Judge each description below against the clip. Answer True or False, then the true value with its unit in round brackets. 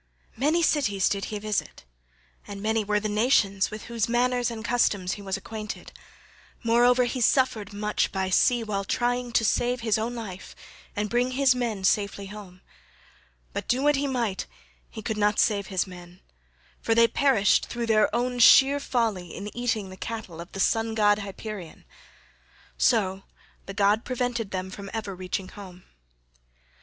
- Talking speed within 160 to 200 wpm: True (165 wpm)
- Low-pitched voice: False (215 Hz)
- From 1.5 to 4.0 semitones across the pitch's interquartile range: True (3.4 semitones)